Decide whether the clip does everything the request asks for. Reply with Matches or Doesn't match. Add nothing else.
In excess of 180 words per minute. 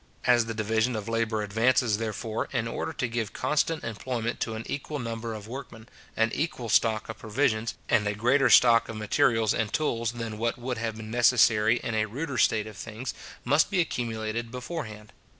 Matches